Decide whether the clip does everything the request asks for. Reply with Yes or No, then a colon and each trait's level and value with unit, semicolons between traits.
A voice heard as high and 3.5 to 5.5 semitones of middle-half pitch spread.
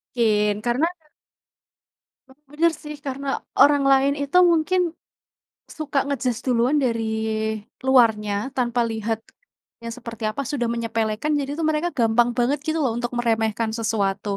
Yes: high, 240 Hz; average, 4.0 semitones